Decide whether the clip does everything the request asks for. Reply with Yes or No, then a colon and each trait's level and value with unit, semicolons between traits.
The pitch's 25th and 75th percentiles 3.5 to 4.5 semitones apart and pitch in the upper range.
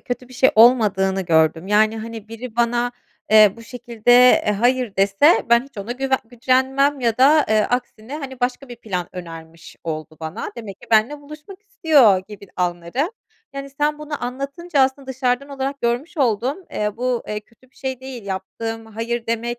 Yes: average, 4.0 semitones; high, 240 Hz